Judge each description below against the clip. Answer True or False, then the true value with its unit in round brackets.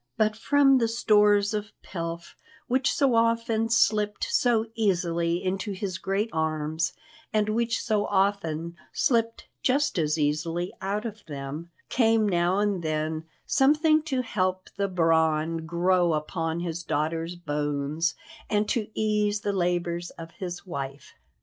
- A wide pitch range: False (4.8 semitones)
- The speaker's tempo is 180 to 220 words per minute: False (135 wpm)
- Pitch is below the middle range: False (185 Hz)